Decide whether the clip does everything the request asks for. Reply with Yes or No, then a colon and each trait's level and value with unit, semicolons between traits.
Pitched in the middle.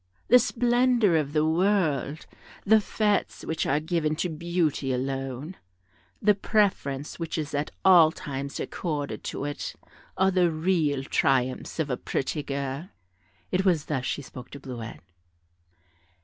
Yes: medium, 155 Hz